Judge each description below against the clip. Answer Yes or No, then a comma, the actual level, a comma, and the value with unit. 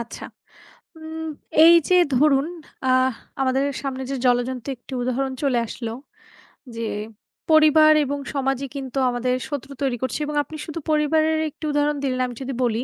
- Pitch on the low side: No, very high, 270 Hz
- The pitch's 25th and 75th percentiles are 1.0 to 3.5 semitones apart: Yes, average, 3.0 semitones